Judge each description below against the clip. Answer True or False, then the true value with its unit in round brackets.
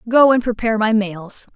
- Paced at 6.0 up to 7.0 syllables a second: False (5.3 syllables/s)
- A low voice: False (220 Hz)